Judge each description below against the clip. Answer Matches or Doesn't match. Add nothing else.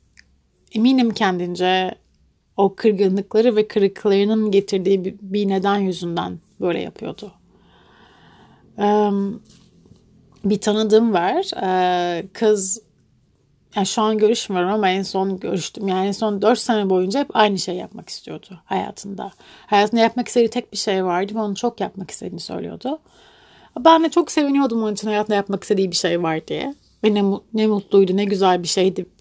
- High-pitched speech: Matches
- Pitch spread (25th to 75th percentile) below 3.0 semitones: Matches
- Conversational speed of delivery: Doesn't match